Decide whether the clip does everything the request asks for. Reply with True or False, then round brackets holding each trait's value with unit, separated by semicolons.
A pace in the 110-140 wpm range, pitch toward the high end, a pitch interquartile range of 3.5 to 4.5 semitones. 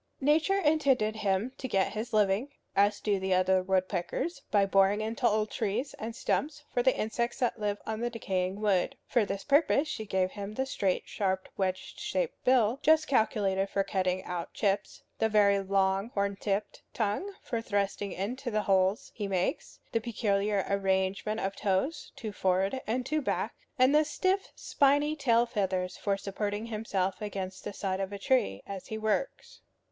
False (175 wpm; 210 Hz; 3.8 semitones)